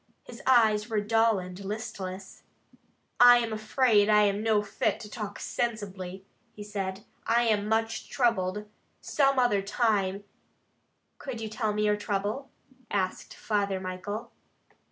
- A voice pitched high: Yes, high, 210 Hz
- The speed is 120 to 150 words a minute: Yes, average, 140 wpm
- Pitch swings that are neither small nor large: No, narrow, 2.2 semitones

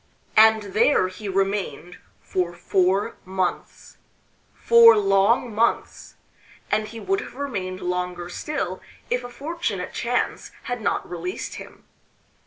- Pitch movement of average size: Yes, average, 4.1 semitones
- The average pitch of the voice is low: No, high, 205 Hz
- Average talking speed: No, slow, 120 wpm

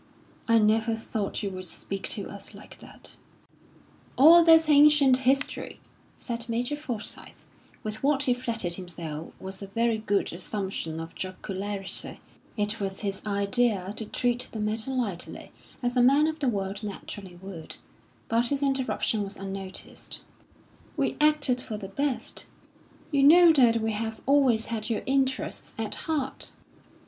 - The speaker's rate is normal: Yes, average, 150 wpm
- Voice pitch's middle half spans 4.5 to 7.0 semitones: Yes, average, 5.2 semitones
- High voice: Yes, high, 225 Hz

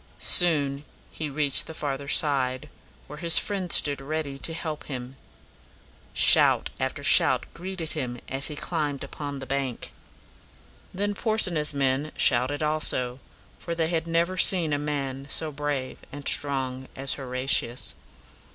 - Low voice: No, medium, 145 Hz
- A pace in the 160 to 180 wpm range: No, average, 140 wpm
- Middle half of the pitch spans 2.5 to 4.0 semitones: Yes, average, 3.1 semitones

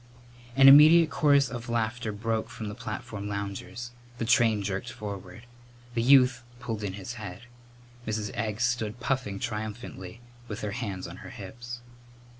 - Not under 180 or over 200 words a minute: No, average, 150 wpm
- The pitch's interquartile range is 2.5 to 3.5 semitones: Yes, average, 2.9 semitones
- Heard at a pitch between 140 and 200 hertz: No, low, 115 Hz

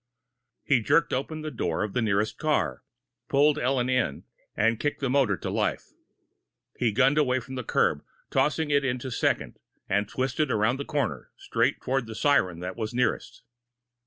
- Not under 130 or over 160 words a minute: No, average, 170 wpm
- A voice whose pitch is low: Yes, low, 130 Hz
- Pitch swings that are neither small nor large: Yes, average, 4.3 semitones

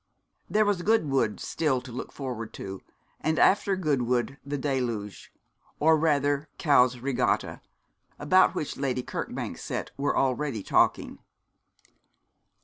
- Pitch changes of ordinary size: Yes, average, 3.7 semitones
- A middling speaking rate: No, slow, 120 wpm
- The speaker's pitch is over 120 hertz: Yes, medium, 140 Hz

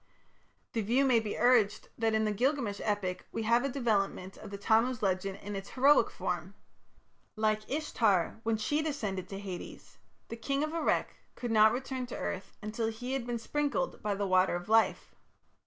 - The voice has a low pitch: No, high, 220 Hz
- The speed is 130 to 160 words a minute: No, average, 185 wpm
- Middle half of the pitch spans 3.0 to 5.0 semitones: Yes, average, 3.9 semitones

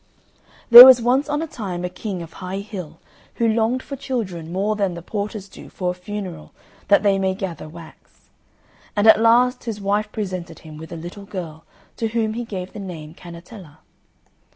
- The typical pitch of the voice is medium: No, high, 195 Hz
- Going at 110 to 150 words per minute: No, average, 190 wpm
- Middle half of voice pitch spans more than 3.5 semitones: Yes, average, 4.2 semitones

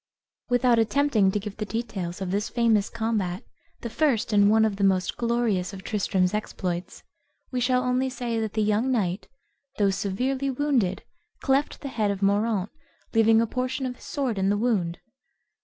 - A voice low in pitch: No, high, 220 Hz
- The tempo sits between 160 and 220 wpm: Yes, average, 175 wpm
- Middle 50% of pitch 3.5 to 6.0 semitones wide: Yes, average, 3.9 semitones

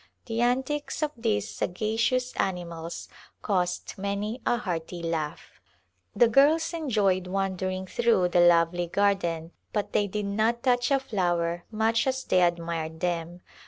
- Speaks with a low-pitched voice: No, high, 195 Hz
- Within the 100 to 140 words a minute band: Yes, slow, 135 wpm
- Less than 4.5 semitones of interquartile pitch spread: No, average, 5.3 semitones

